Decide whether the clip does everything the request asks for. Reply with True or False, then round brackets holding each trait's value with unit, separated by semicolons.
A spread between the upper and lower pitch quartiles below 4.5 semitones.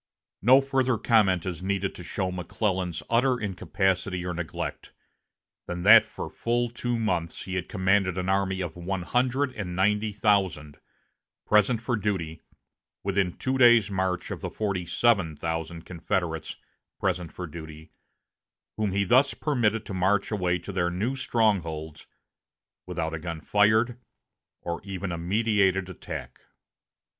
True (3.7 semitones)